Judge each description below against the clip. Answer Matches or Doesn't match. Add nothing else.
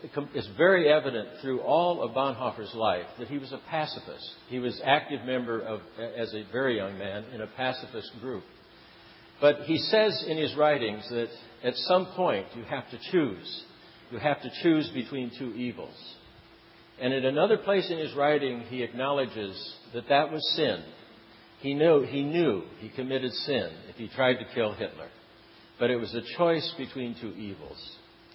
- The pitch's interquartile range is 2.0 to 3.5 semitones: Doesn't match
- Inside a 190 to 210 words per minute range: Doesn't match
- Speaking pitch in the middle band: Doesn't match